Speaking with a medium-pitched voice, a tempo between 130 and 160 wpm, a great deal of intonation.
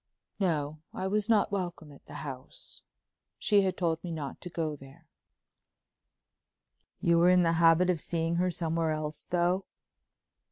No: medium, 170 Hz; average, 150 wpm; narrow, 2.6 semitones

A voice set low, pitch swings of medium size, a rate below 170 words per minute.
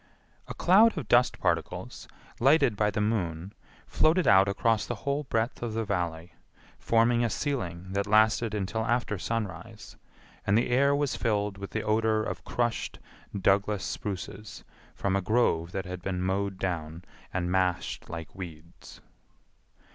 Yes: low, 105 Hz; average, 3.9 semitones; average, 150 wpm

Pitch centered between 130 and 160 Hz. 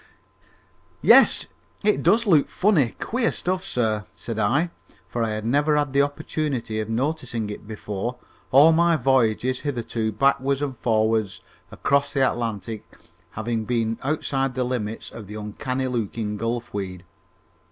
No: low, 120 Hz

